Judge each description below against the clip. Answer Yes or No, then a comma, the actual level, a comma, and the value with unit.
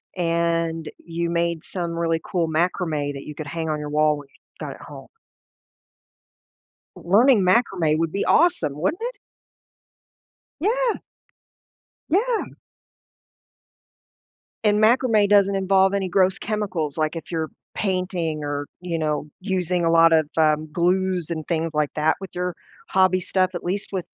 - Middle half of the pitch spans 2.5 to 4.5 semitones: Yes, average, 3.4 semitones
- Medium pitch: Yes, medium, 170 Hz